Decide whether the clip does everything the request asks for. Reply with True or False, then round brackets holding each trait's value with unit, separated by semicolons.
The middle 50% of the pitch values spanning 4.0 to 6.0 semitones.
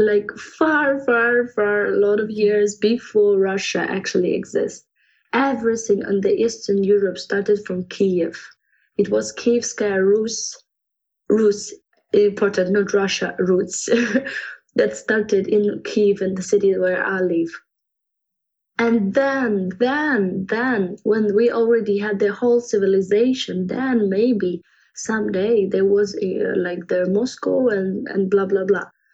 False (2.9 semitones)